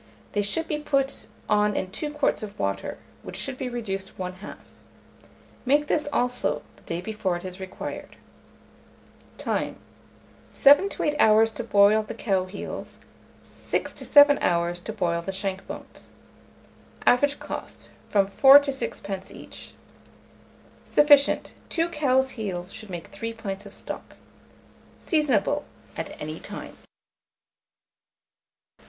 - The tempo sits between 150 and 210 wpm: No, slow, 135 wpm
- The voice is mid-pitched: No, high, 215 Hz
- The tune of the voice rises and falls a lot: Yes, wide, 6.3 semitones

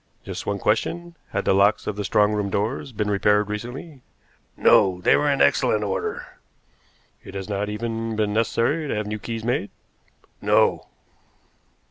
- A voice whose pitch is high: No, low, 105 Hz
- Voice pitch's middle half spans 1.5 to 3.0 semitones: Yes, narrow, 2.4 semitones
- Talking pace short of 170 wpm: Yes, average, 160 wpm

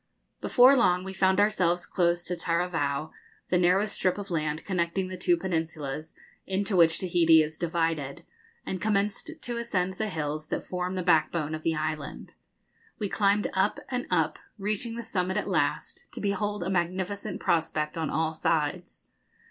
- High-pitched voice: No, medium, 180 Hz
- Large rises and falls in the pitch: No, average, 3.5 semitones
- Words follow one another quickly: No, average, 165 wpm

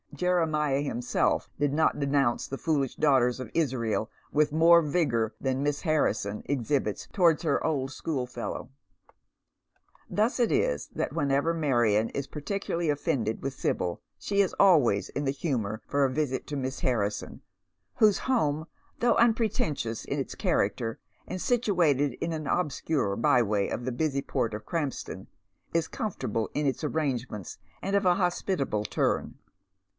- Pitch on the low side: No, medium, 145 Hz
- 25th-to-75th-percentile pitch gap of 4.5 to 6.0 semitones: Yes, average, 4.9 semitones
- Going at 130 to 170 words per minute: Yes, average, 150 wpm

